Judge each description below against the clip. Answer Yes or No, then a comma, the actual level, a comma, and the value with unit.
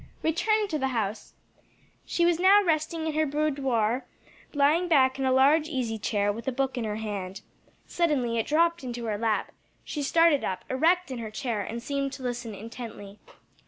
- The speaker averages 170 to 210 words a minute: Yes, average, 185 wpm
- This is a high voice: Yes, very high, 265 Hz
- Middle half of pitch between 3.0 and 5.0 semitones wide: No, wide, 5.6 semitones